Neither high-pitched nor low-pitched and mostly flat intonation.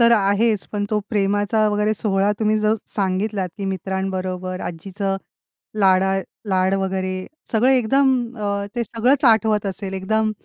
No: high, 200 Hz; narrow, 2.3 semitones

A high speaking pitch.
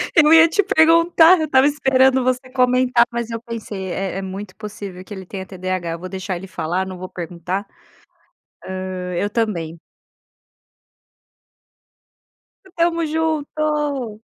Yes: high, 220 Hz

